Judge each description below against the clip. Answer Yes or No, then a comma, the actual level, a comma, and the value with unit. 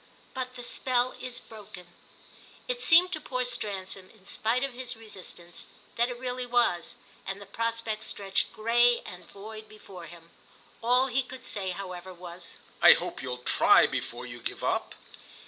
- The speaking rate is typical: Yes, average, 165 wpm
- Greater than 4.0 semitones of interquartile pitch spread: Yes, average, 4.8 semitones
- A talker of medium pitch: No, high, 220 Hz